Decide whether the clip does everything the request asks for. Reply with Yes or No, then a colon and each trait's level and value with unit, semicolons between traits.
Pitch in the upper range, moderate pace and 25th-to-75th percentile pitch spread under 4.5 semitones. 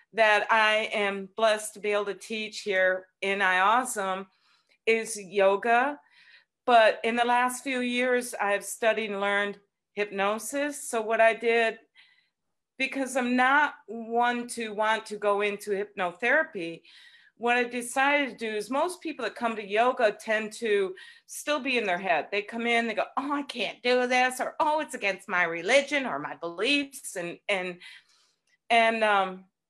Yes: high, 225 Hz; average, 165 wpm; average, 3.9 semitones